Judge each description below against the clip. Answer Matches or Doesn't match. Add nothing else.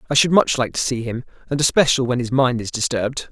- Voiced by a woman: Doesn't match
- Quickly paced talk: Matches